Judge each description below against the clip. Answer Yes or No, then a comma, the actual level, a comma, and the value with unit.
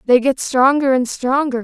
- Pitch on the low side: No, very high, 260 Hz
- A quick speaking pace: No, average, 185 wpm